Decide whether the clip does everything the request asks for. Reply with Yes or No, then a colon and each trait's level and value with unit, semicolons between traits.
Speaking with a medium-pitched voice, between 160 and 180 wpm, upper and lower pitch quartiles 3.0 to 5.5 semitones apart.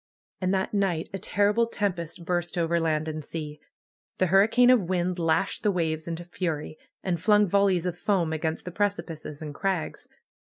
Yes: medium, 175 Hz; average, 170 wpm; average, 3.3 semitones